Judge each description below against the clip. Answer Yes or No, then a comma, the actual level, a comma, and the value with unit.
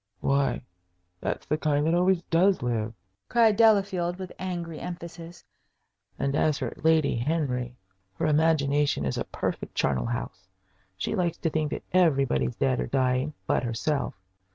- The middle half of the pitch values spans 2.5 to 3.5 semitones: No, wide, 5.6 semitones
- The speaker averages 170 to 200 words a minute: No, average, 150 wpm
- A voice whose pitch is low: No, medium, 150 Hz